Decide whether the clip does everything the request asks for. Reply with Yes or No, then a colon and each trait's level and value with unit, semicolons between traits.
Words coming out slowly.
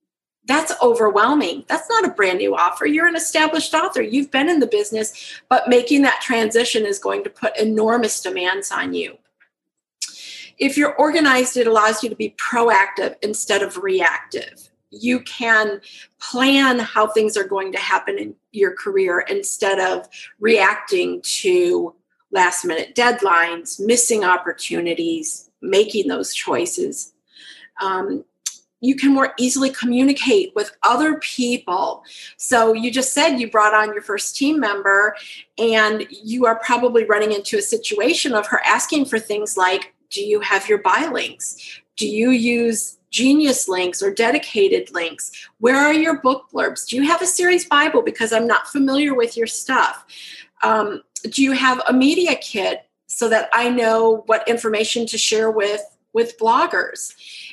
No: average, 155 wpm